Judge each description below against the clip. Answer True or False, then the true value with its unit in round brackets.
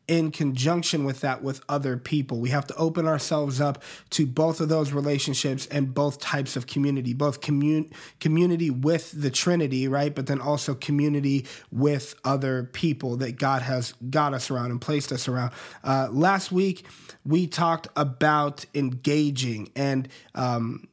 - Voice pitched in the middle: True (145 Hz)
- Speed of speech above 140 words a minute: True (160 wpm)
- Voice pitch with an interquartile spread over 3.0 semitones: False (2.5 semitones)